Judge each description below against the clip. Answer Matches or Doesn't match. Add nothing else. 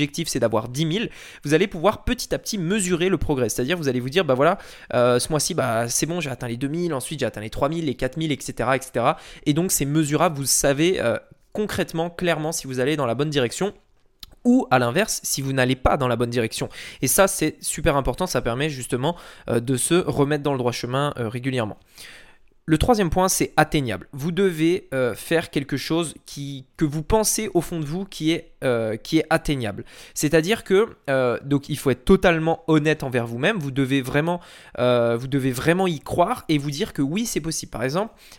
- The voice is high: Doesn't match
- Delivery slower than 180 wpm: Doesn't match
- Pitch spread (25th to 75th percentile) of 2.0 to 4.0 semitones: Doesn't match